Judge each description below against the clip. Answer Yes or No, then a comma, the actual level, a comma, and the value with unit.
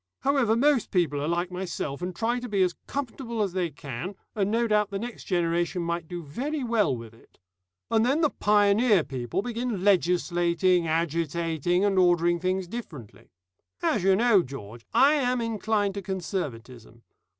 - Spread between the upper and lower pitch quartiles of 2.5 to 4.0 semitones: No, average, 4.9 semitones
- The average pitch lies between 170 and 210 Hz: Yes, medium, 185 Hz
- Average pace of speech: Yes, average, 165 wpm